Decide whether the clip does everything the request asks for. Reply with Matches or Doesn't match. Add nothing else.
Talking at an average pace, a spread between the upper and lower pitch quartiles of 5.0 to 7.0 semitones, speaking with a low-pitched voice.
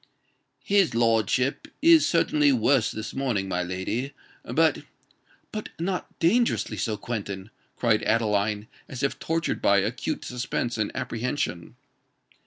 Doesn't match